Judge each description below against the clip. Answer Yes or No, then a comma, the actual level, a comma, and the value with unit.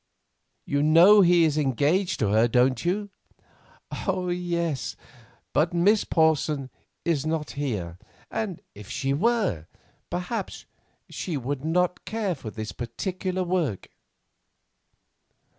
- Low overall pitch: No, medium, 160 Hz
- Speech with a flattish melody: No, average, 5.2 semitones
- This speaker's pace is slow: Yes, slow, 110 wpm